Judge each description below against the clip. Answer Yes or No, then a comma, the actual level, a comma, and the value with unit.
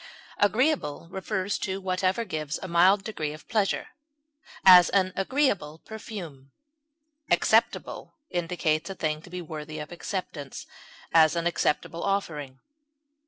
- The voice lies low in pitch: No, medium, 175 Hz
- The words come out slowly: Yes, slow, 120 wpm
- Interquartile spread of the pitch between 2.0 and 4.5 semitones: Yes, average, 4.0 semitones